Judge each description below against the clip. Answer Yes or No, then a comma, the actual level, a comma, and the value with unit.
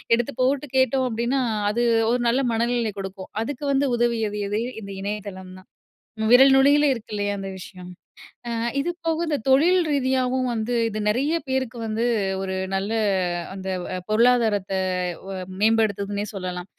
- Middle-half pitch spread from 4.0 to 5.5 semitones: Yes, average, 4.5 semitones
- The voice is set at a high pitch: Yes, high, 230 Hz